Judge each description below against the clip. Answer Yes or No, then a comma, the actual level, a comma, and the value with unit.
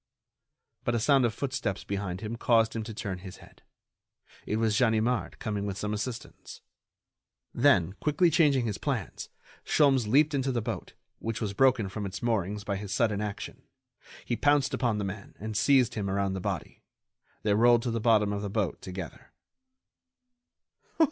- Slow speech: No, average, 170 wpm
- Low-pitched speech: Yes, low, 110 Hz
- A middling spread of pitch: Yes, average, 3.3 semitones